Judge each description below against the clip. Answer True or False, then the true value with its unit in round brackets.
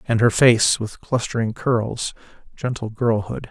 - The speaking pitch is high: False (115 Hz)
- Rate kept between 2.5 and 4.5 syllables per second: True (4.1 syllables/s)